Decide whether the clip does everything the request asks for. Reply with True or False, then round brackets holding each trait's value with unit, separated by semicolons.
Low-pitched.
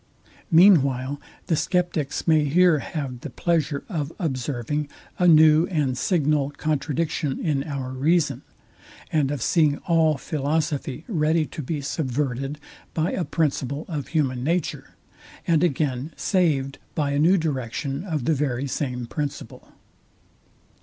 False (150 Hz)